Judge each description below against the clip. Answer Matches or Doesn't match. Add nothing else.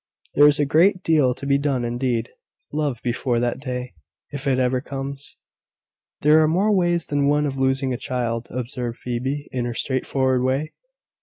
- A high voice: Doesn't match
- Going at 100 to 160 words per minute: Doesn't match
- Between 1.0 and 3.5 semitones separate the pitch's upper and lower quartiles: Matches